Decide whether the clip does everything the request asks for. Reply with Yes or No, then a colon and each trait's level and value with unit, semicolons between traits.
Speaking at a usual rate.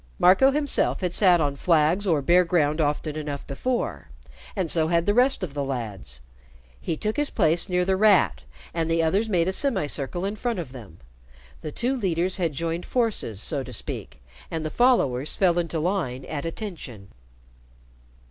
Yes: average, 175 wpm